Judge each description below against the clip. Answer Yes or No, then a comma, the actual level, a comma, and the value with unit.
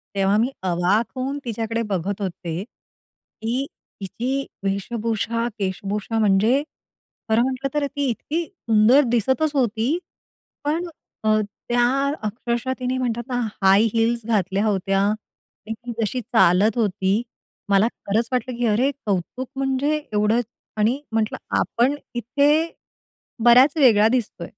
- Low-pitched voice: No, high, 230 Hz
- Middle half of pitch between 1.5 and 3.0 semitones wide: No, average, 3.7 semitones